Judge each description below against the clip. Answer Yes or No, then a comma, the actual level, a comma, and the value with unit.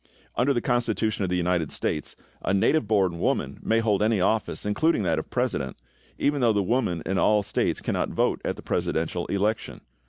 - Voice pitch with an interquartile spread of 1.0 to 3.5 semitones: No, average, 3.9 semitones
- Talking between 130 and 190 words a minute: No, average, 200 wpm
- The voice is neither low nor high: No, low, 105 Hz